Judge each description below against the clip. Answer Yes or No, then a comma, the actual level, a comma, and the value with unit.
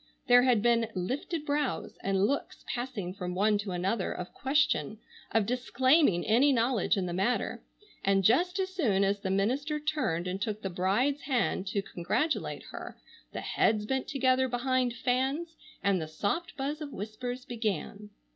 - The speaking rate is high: No, average, 165 wpm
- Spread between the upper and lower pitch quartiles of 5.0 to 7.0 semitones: Yes, wide, 5.4 semitones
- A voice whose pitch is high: Yes, high, 235 Hz